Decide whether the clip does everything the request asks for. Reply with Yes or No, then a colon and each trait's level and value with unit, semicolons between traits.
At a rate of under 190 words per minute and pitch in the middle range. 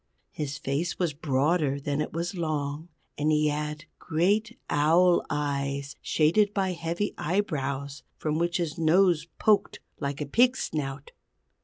Yes: average, 140 wpm; medium, 155 Hz